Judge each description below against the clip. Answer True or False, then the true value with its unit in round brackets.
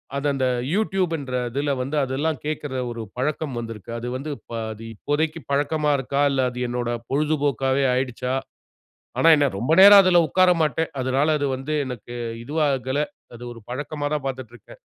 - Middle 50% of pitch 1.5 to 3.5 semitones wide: True (3.2 semitones)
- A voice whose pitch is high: False (140 Hz)